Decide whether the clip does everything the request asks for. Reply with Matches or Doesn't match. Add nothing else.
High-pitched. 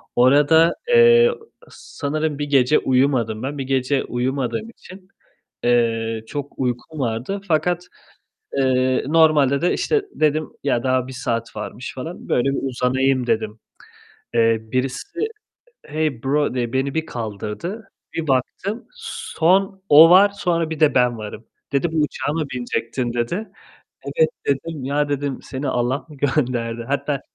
Doesn't match